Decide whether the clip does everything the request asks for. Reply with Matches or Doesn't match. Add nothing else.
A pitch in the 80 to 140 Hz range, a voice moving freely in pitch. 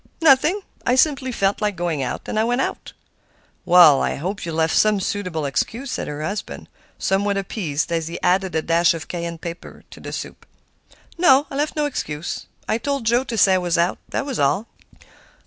Doesn't match